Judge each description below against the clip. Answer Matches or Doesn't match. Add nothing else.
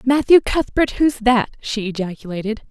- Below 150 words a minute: Matches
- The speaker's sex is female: Matches